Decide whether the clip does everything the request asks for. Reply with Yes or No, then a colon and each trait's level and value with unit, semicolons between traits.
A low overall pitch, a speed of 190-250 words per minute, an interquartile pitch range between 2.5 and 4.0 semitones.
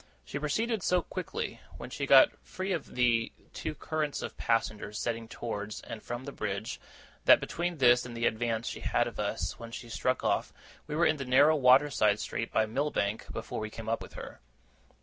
No: low, 125 Hz; average, 200 wpm; average, 4.9 semitones